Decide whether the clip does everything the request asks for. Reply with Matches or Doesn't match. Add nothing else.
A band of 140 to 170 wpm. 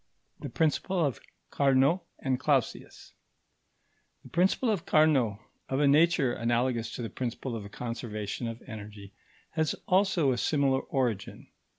Matches